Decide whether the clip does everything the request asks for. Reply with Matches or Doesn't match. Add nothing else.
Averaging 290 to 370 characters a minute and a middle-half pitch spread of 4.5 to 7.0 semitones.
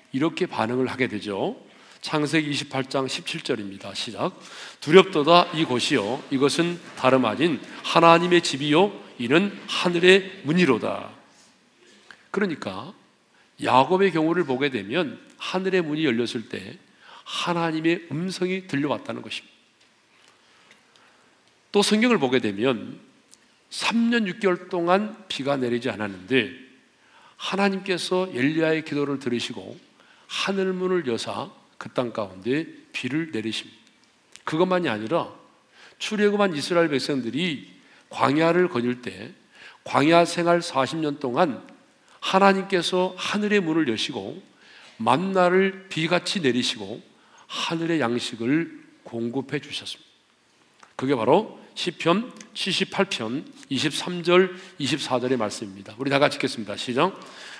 Doesn't match